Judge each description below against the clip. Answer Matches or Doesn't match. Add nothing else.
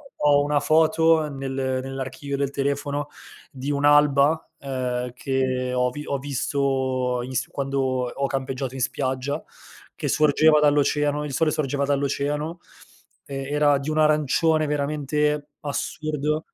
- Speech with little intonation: Matches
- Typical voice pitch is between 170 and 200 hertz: Doesn't match